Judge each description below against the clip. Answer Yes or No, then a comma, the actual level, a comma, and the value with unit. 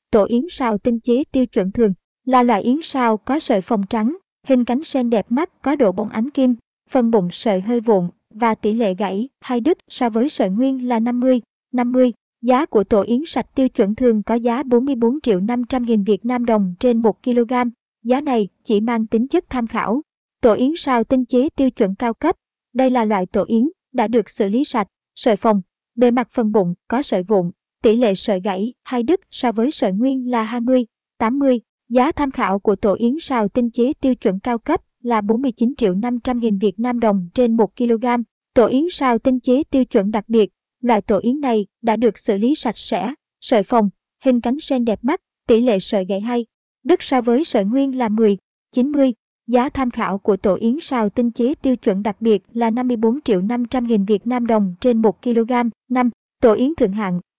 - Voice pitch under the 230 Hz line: No, high, 240 Hz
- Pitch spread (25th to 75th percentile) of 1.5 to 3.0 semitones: Yes, narrow, 2.6 semitones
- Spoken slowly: No, average, 215 wpm